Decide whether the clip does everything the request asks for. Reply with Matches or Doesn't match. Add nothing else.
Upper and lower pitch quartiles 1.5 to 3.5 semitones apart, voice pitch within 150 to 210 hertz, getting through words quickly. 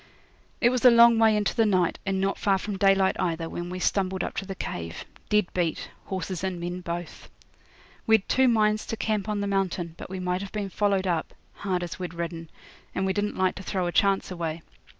Matches